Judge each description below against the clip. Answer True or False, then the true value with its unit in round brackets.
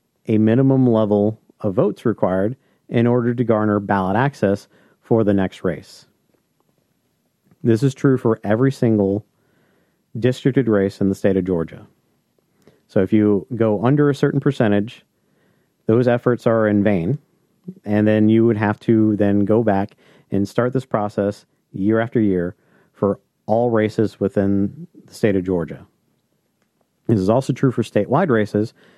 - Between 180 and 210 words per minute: False (150 wpm)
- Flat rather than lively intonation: False (3.5 semitones)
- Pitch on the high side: False (110 Hz)